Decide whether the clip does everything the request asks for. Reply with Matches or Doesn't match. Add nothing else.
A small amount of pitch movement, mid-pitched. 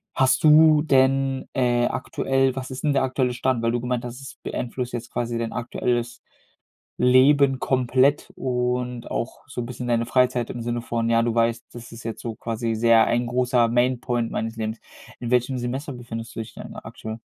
Doesn't match